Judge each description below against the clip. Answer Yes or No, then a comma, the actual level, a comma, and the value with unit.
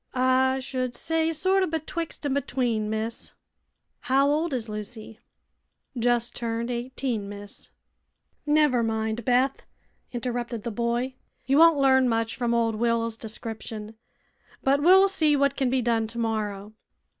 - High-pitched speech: Yes, high, 245 Hz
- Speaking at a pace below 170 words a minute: Yes, slow, 135 wpm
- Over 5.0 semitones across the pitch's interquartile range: No, average, 3.4 semitones